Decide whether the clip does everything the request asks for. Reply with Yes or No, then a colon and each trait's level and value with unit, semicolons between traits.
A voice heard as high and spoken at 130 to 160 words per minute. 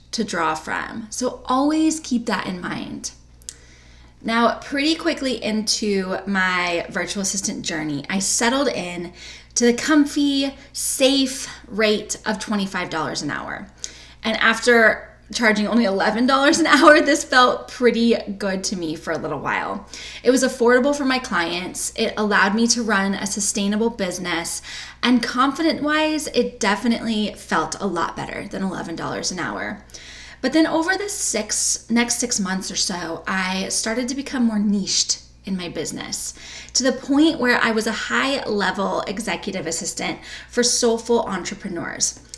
Yes: high, 220 Hz; average, 145 wpm